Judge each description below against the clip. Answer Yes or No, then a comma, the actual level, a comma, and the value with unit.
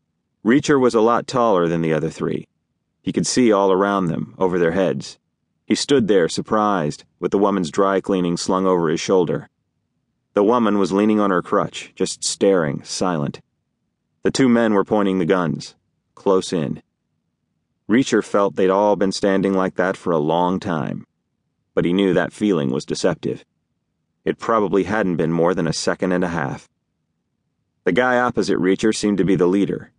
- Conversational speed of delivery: Yes, average, 180 wpm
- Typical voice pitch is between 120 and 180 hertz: No, very low, 95 Hz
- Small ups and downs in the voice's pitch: Yes, narrow, 2.0 semitones